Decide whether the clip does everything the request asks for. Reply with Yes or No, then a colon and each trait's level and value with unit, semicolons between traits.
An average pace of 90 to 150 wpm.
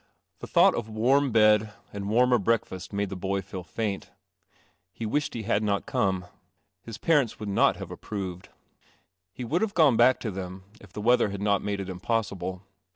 No: average, 190 wpm